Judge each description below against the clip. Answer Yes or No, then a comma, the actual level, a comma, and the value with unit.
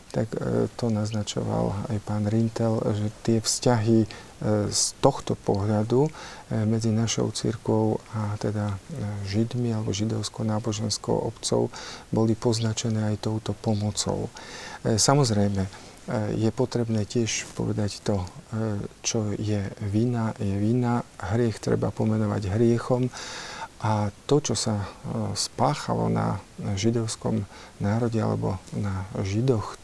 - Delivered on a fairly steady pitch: Yes, narrow, 1.7 semitones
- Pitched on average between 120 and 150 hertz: No, low, 110 Hz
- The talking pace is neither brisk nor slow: No, slow, 105 wpm